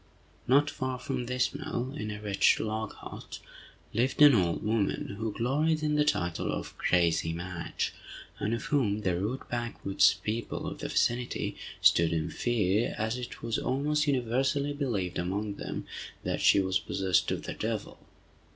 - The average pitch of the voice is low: Yes, low, 115 Hz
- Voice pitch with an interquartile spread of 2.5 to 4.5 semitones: No, average, 5.1 semitones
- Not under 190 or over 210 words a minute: No, average, 160 wpm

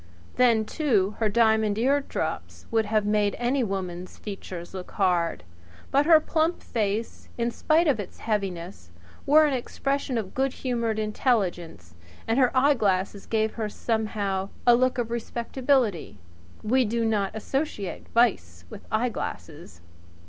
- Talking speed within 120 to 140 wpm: Yes, slow, 135 wpm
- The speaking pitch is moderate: No, high, 220 Hz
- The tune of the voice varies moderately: Yes, average, 4.2 semitones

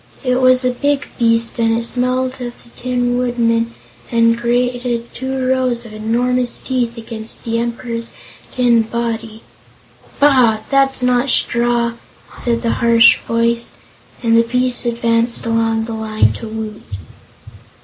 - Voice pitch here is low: No, high, 235 Hz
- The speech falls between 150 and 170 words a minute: No, average, 140 wpm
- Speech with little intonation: Yes, narrow, 1.5 semitones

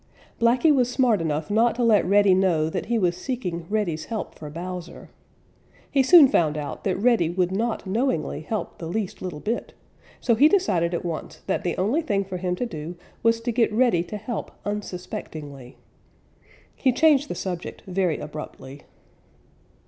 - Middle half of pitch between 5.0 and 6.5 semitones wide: Yes, wide, 5.6 semitones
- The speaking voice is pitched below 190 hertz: No, high, 195 Hz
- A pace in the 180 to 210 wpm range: No, average, 170 wpm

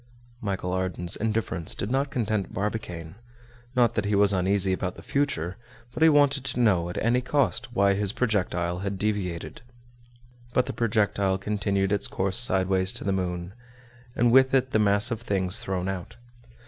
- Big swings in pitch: No, average, 3.9 semitones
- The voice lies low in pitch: Yes, low, 100 Hz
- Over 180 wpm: No, average, 170 wpm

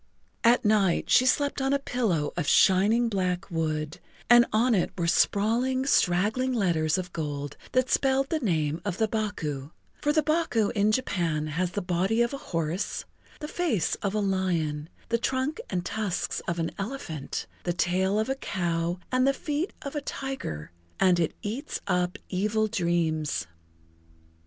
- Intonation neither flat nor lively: No, wide, 6.6 semitones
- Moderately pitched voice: No, high, 200 Hz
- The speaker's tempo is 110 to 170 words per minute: Yes, average, 165 wpm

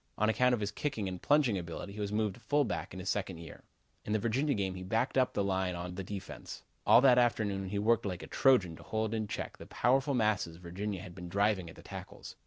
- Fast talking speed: Yes, fast, 245 wpm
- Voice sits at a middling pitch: No, low, 105 Hz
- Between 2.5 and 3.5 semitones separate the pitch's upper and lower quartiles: No, average, 3.9 semitones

